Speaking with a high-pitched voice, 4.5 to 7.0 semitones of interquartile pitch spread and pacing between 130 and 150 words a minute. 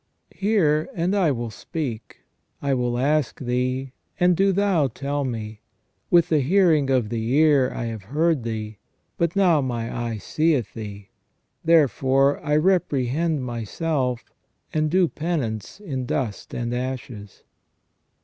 No: low, 135 Hz; average, 5.3 semitones; slow, 135 wpm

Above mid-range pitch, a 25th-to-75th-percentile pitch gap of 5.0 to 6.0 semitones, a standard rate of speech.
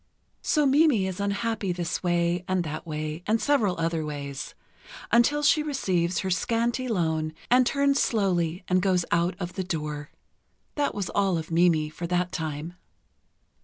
No: medium, 180 Hz; average, 5.3 semitones; average, 160 wpm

